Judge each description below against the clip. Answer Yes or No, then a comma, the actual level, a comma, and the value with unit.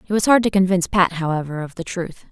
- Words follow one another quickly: Yes, fast, 260 wpm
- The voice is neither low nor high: Yes, medium, 180 Hz